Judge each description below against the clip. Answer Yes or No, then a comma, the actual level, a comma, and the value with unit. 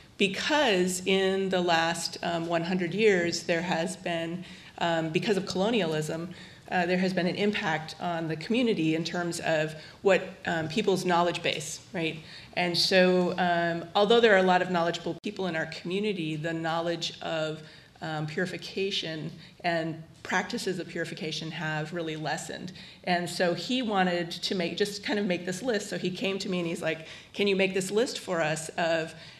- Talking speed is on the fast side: No, average, 175 wpm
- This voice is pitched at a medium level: Yes, medium, 175 Hz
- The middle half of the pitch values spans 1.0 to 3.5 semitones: Yes, narrow, 2.6 semitones